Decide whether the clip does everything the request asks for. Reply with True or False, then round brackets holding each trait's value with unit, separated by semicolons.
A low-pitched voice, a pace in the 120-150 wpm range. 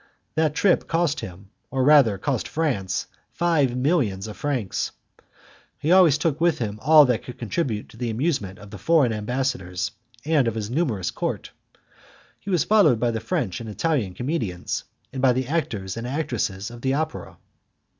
False (125 Hz; 175 wpm)